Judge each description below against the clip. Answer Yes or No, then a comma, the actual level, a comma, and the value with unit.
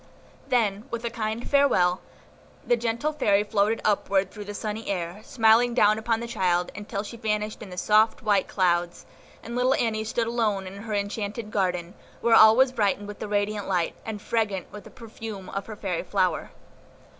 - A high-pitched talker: Yes, high, 210 Hz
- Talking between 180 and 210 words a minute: Yes, average, 185 wpm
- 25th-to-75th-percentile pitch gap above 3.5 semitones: No, narrow, 2.4 semitones